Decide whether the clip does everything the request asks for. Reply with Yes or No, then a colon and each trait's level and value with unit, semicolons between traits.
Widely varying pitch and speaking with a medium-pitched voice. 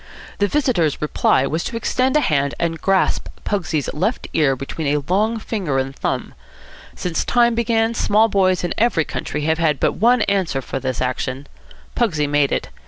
Yes: wide, 7.4 semitones; medium, 170 Hz